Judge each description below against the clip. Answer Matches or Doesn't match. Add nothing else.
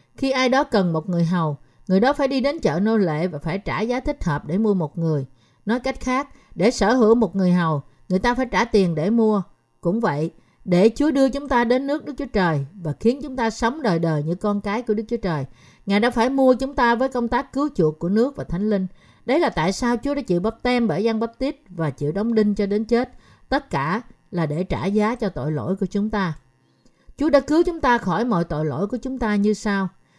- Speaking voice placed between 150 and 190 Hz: Doesn't match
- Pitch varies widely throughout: Matches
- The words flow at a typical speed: Doesn't match